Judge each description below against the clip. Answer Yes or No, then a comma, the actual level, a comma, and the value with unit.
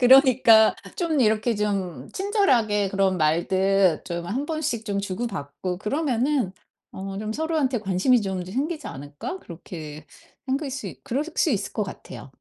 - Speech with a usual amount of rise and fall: No, wide, 6.1 semitones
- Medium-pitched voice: No, high, 210 Hz